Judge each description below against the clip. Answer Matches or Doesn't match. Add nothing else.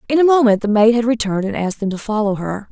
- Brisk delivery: Matches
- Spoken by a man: Doesn't match